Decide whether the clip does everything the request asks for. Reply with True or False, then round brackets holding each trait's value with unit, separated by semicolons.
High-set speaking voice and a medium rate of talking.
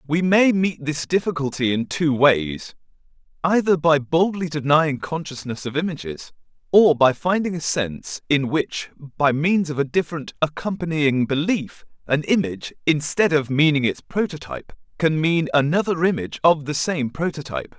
False (155 Hz; 150 wpm)